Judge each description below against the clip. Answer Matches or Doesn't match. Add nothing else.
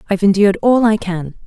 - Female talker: Matches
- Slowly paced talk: Doesn't match